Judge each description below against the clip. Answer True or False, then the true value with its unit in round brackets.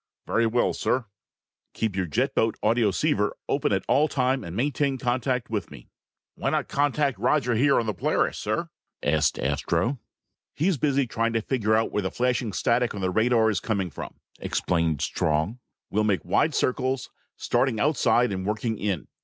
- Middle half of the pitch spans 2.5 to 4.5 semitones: True (4.2 semitones)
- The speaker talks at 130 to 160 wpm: False (170 wpm)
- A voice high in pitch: False (115 Hz)